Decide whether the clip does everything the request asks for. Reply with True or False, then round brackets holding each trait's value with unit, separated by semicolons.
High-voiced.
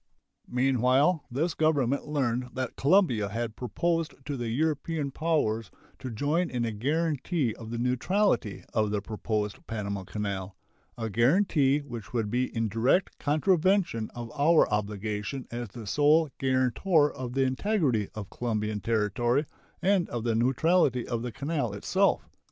False (125 Hz)